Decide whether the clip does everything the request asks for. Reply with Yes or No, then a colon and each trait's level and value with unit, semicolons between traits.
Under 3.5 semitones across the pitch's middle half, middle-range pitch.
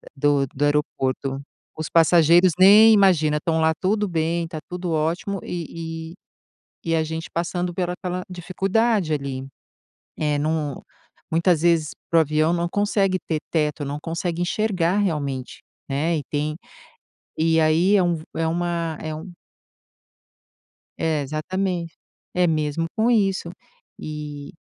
Yes: average, 2.8 semitones; medium, 165 Hz